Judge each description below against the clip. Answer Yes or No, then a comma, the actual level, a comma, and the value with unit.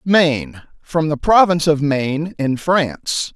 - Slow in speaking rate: Yes, slow, 125 wpm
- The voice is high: No, medium, 155 Hz